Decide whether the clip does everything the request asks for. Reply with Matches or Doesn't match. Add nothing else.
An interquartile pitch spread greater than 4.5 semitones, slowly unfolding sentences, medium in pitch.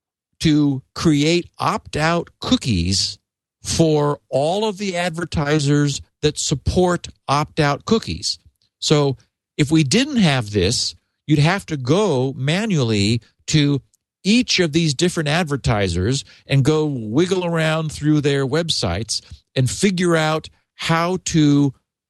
Matches